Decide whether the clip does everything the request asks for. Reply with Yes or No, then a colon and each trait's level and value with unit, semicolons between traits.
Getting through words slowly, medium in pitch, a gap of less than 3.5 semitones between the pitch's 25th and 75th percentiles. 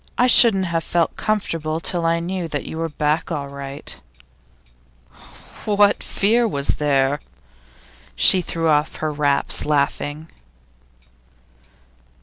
No: slow, 120 wpm; medium, 160 Hz; average, 3.8 semitones